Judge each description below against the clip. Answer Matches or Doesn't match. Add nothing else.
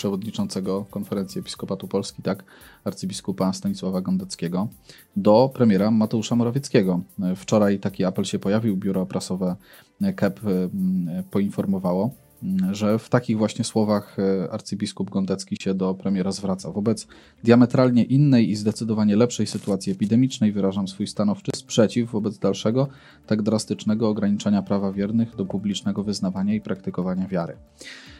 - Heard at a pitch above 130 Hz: Doesn't match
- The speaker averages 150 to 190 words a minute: Doesn't match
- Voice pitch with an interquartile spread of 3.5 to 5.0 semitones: Matches